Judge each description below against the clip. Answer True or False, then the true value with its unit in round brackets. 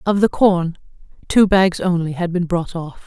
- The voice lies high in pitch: False (180 Hz)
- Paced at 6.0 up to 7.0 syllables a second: False (4.5 syllables/s)